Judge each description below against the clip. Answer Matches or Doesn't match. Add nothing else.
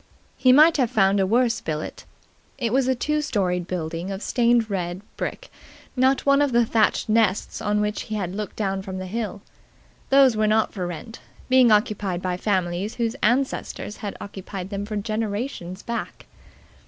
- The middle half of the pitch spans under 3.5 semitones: Doesn't match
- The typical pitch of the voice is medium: Doesn't match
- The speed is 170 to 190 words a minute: Matches